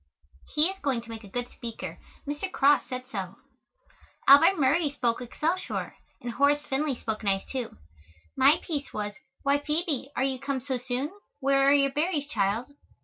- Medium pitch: No, very high, 275 Hz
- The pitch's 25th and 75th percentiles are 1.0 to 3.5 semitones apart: Yes, average, 3.2 semitones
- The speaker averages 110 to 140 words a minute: No, average, 170 wpm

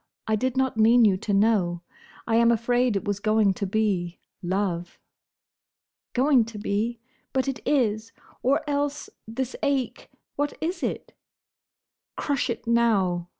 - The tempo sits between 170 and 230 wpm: No, average, 140 wpm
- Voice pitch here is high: Yes, high, 225 Hz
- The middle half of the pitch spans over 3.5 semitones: Yes, average, 4.1 semitones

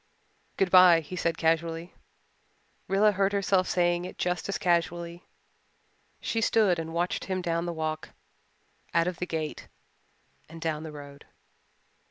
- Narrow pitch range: Yes, narrow, 2.0 semitones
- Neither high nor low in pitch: Yes, medium, 170 Hz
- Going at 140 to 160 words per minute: Yes, average, 145 wpm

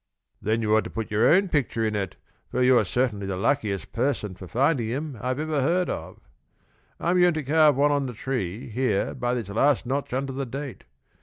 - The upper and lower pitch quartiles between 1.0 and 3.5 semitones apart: No, average, 4.7 semitones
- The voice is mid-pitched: No, low, 125 Hz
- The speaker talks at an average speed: No, fast, 210 wpm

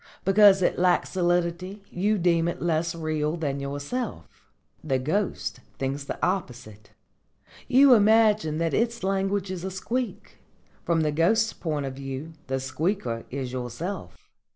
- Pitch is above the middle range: No, medium, 170 Hz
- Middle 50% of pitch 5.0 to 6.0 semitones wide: Yes, wide, 5.6 semitones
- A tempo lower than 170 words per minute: Yes, average, 140 wpm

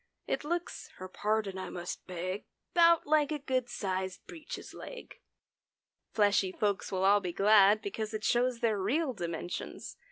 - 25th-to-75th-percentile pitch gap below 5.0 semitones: No, wide, 5.5 semitones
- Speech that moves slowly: No, average, 155 wpm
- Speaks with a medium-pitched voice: No, high, 210 Hz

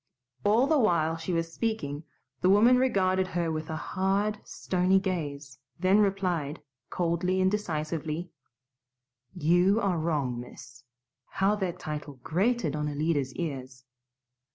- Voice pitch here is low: No, medium, 175 Hz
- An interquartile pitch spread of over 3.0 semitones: Yes, average, 4.1 semitones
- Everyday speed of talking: No, slow, 130 wpm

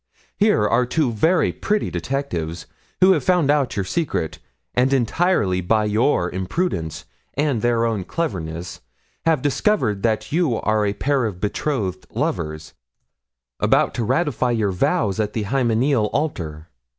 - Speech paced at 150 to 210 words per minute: No, average, 140 wpm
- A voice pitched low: Yes, low, 115 Hz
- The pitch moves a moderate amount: No, wide, 6.8 semitones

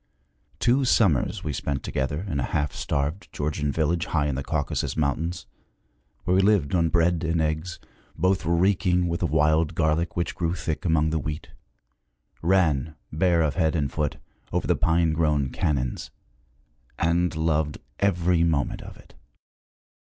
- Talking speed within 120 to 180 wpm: Yes, average, 155 wpm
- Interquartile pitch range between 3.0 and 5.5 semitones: No, narrow, 2.4 semitones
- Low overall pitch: Yes, very low, 80 Hz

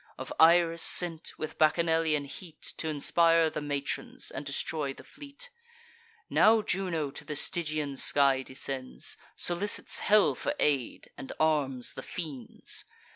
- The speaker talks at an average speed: No, slow, 130 wpm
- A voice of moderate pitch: Yes, medium, 155 Hz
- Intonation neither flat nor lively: Yes, average, 3.3 semitones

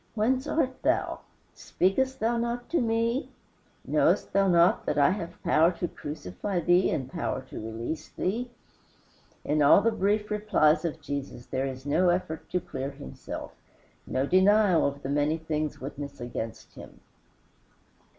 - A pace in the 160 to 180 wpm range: No, average, 150 wpm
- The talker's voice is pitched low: No, medium, 170 Hz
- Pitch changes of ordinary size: No, wide, 6.7 semitones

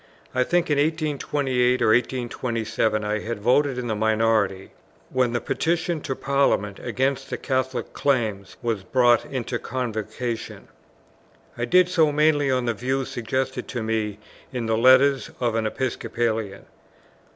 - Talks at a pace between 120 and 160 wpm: Yes, average, 140 wpm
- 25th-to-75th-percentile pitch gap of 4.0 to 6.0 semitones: No, average, 3.3 semitones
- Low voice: Yes, low, 125 Hz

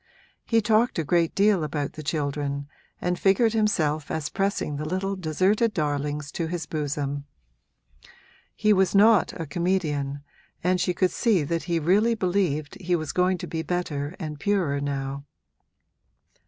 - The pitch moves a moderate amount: Yes, average, 4.7 semitones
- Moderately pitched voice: Yes, medium, 170 Hz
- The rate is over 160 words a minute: No, average, 155 wpm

